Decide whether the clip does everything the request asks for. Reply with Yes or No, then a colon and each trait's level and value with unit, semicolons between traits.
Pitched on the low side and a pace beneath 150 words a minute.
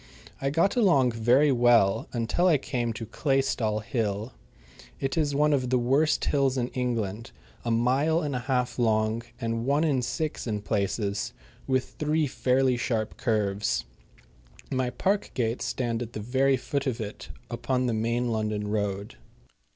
No: low, 125 Hz; average, 160 wpm